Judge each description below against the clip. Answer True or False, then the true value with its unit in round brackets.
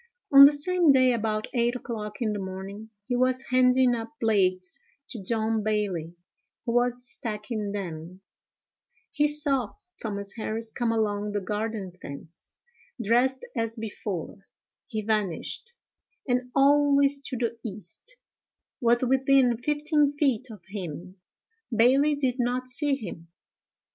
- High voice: True (230 Hz)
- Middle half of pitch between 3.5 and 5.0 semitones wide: True (4.0 semitones)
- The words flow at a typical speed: False (130 wpm)